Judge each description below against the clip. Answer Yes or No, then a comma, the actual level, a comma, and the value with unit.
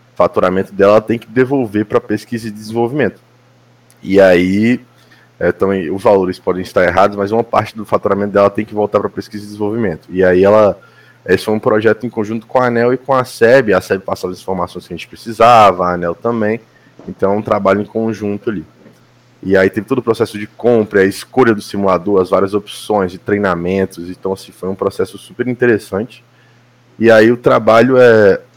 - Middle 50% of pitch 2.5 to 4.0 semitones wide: Yes, average, 3.3 semitones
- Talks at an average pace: No, fast, 200 wpm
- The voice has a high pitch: No, low, 105 Hz